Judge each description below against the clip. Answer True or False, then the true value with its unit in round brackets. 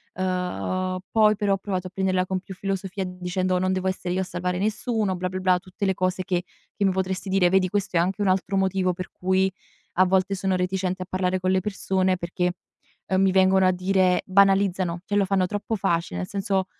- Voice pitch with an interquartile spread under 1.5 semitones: True (1.0 semitones)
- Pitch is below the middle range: False (185 Hz)